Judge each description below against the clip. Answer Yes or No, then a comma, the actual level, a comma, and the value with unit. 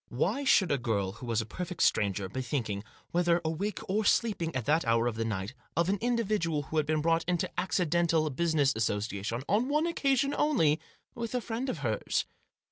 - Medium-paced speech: Yes, average, 195 wpm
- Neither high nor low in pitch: Yes, medium, 160 Hz